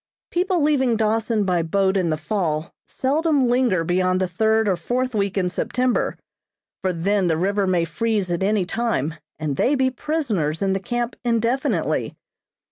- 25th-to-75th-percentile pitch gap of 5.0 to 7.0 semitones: Yes, average, 5.3 semitones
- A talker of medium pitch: No, high, 205 Hz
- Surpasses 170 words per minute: No, average, 165 wpm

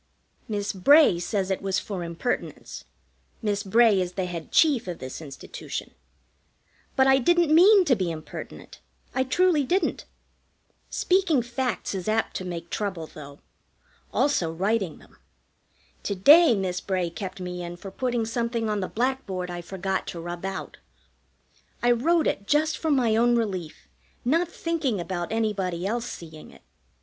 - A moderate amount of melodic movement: No, wide, 6.4 semitones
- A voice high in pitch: Yes, high, 205 Hz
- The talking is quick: No, average, 155 wpm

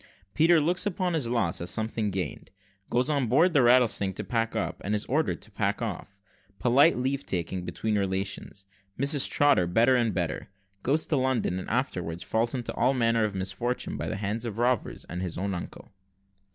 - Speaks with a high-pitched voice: No, low, 115 Hz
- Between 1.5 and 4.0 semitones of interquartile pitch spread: No, average, 5.1 semitones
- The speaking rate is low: No, average, 190 wpm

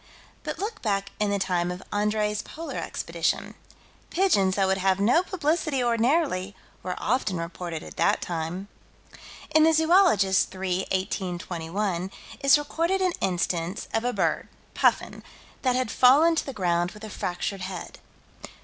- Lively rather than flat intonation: Yes, wide, 7.1 semitones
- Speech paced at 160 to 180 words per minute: No, average, 150 wpm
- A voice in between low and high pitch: No, high, 205 Hz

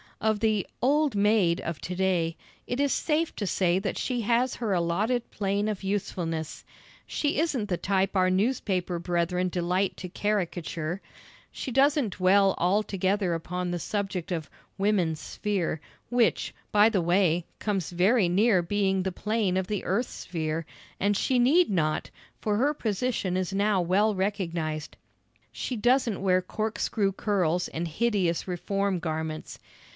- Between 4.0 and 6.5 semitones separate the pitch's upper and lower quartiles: No, average, 3.4 semitones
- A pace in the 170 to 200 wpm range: No, average, 150 wpm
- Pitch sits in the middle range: No, high, 195 Hz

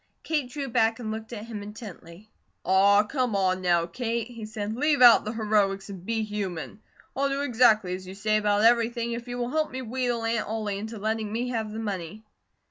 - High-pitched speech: Yes, high, 220 Hz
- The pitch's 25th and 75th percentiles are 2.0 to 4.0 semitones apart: Yes, average, 2.7 semitones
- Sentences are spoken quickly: Yes, fast, 210 wpm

